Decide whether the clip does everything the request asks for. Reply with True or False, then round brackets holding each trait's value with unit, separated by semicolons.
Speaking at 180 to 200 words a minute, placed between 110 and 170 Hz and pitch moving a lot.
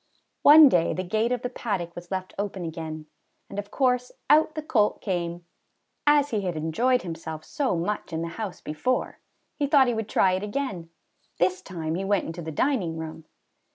False (190 wpm; 190 Hz; 6.8 semitones)